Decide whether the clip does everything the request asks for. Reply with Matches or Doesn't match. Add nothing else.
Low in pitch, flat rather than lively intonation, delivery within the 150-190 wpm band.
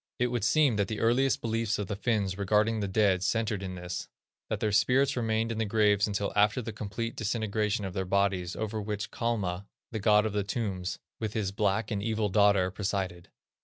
Doesn't match